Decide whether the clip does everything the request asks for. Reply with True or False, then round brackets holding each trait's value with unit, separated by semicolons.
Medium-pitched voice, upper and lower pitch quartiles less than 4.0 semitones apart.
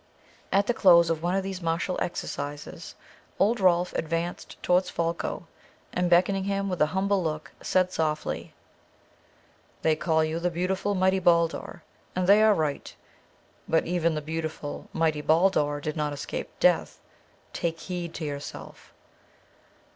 True (170 Hz; 2.8 semitones)